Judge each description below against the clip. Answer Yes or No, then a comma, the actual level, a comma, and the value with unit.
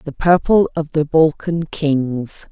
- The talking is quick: No, average, 145 wpm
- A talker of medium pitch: Yes, medium, 155 Hz